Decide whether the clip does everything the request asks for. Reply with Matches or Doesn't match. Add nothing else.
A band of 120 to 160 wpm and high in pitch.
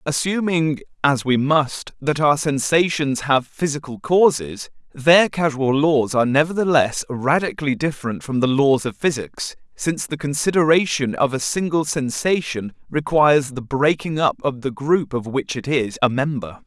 Doesn't match